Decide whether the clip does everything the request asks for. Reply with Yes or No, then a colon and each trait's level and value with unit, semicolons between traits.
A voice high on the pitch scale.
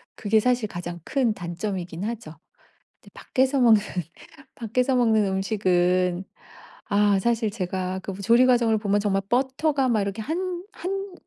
Yes: high, 215 Hz